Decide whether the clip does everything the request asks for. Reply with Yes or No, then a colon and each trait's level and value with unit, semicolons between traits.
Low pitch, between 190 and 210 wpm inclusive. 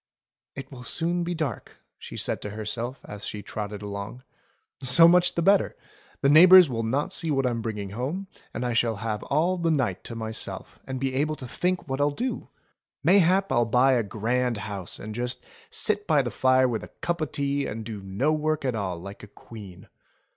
Yes: low, 125 Hz; fast, 205 wpm